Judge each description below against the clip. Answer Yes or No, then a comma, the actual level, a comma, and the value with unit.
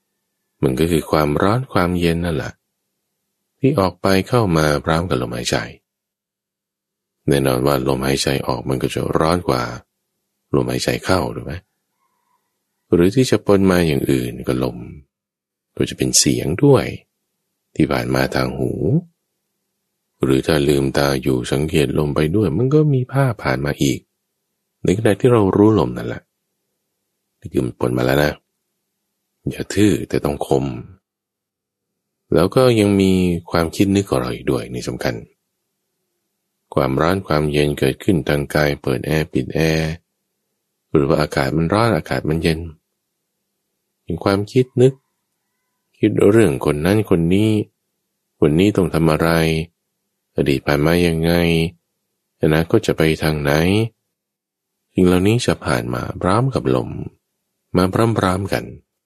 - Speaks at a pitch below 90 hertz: Yes, very low, 80 Hz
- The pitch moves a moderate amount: No, wide, 6.9 semitones